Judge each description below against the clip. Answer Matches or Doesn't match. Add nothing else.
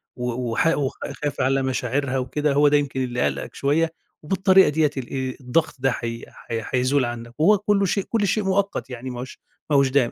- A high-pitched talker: Doesn't match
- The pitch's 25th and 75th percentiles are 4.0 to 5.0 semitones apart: Matches